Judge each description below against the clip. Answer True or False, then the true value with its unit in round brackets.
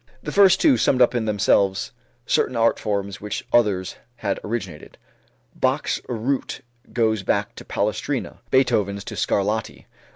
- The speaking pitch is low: True (110 Hz)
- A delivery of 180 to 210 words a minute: False (135 wpm)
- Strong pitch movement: False (3.3 semitones)